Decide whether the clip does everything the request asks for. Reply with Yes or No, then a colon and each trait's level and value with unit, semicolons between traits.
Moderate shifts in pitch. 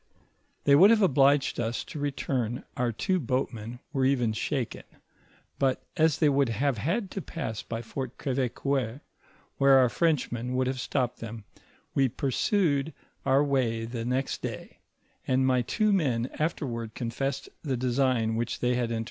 Yes: average, 3.1 semitones